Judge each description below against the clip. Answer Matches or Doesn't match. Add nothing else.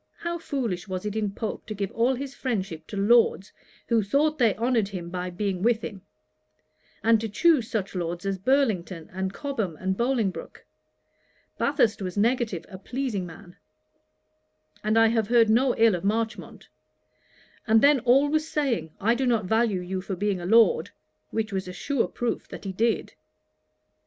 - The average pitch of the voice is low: Doesn't match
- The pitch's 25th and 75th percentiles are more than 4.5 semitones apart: Doesn't match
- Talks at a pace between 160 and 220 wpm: Matches